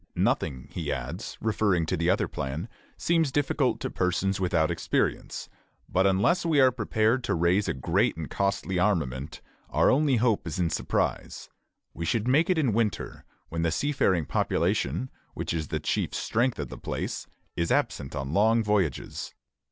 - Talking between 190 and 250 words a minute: No, average, 165 wpm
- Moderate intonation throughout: No, wide, 6.1 semitones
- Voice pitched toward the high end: No, very low, 95 Hz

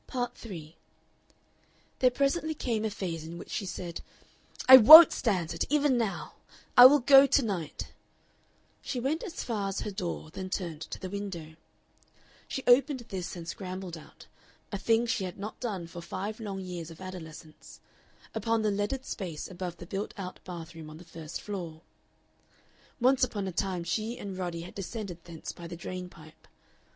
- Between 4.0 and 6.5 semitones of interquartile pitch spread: Yes, average, 5.0 semitones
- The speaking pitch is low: No, high, 190 Hz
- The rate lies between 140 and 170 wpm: No, average, 180 wpm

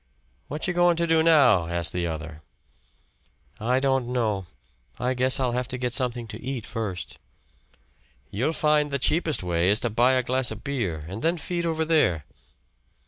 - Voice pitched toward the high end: No, low, 125 Hz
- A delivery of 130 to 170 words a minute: No, average, 180 wpm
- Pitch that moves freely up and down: Yes, wide, 6.4 semitones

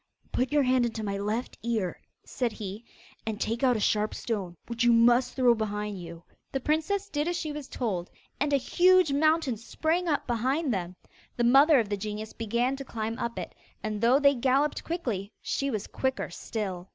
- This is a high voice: Yes, high, 240 Hz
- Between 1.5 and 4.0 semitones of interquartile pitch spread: No, average, 4.7 semitones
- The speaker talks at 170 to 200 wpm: Yes, average, 195 wpm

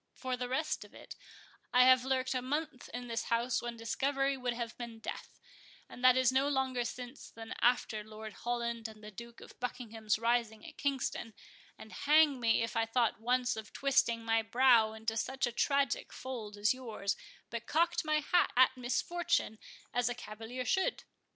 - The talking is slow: No, average, 185 wpm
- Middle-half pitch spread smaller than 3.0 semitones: Yes, narrow, 2.5 semitones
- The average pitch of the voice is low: No, high, 245 Hz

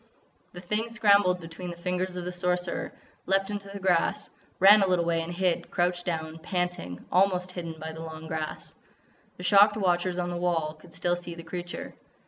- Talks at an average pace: Yes, average, 190 wpm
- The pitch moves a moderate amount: No, narrow, 1.8 semitones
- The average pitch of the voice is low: No, medium, 180 Hz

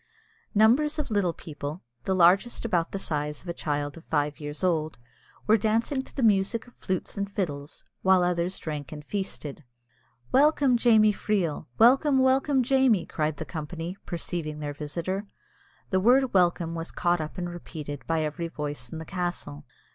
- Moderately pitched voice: Yes, medium, 175 Hz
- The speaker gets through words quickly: No, average, 170 wpm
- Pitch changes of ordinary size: No, wide, 5.9 semitones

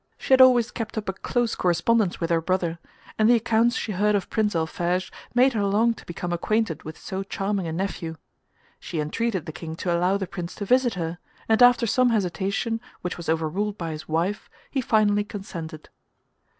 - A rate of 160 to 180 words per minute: No, average, 195 wpm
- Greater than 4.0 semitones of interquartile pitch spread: Yes, average, 4.7 semitones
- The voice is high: Yes, high, 195 Hz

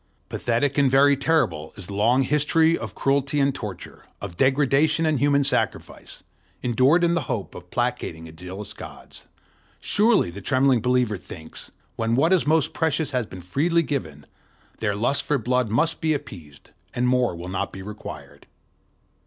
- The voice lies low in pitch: Yes, low, 125 Hz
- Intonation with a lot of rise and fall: Yes, wide, 6.2 semitones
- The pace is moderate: Yes, average, 165 wpm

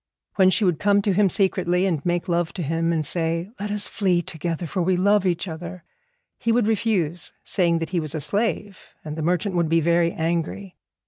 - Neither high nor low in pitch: Yes, medium, 175 Hz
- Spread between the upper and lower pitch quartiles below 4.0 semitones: Yes, average, 3.0 semitones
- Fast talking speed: Yes, fast, 210 wpm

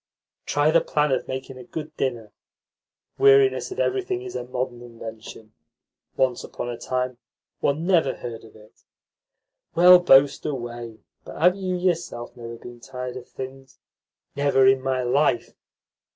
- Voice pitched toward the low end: Yes, low, 130 Hz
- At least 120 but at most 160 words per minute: Yes, average, 150 wpm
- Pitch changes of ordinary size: Yes, average, 4.7 semitones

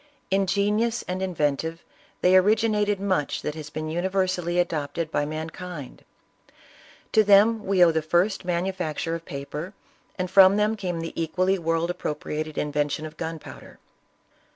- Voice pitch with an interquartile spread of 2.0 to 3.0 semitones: No, average, 3.5 semitones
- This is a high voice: No, medium, 175 Hz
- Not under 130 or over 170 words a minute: Yes, average, 145 wpm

